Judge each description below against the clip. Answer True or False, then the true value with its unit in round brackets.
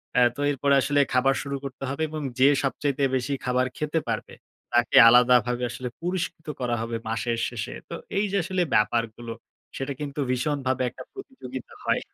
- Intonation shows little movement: False (3.1 semitones)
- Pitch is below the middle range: True (130 Hz)